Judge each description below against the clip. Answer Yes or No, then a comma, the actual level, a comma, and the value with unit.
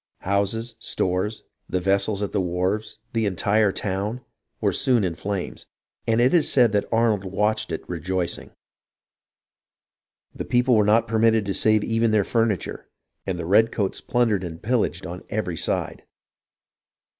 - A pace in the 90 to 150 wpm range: Yes, average, 145 wpm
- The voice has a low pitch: Yes, low, 105 Hz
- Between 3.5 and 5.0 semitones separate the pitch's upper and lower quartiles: No, average, 3.1 semitones